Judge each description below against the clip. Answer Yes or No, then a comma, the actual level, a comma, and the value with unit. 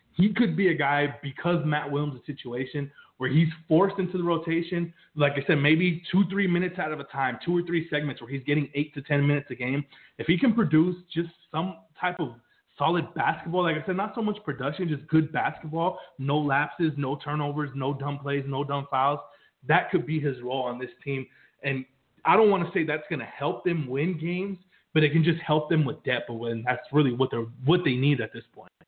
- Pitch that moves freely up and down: No, average, 3.7 semitones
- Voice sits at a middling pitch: Yes, medium, 150 Hz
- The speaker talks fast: Yes, fast, 230 wpm